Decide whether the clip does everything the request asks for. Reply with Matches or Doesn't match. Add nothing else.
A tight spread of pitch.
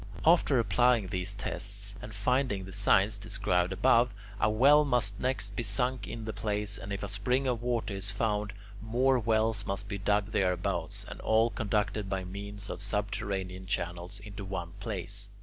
Matches